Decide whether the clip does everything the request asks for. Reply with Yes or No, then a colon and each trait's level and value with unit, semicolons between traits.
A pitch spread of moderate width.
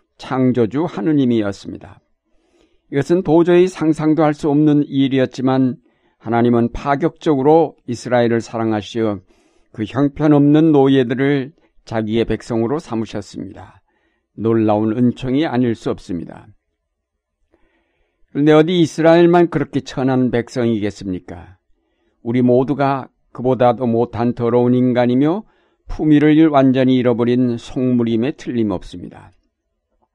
Yes: average, 4.3 semitones